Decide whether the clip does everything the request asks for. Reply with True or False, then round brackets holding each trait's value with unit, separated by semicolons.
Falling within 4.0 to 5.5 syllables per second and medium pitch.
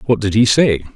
False (5.1 syllables/s; 110 Hz)